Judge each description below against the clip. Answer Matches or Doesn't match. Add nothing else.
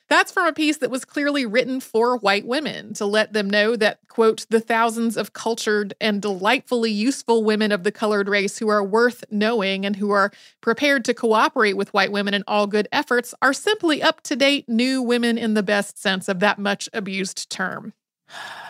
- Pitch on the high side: Matches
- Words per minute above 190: Matches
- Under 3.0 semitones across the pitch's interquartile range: Doesn't match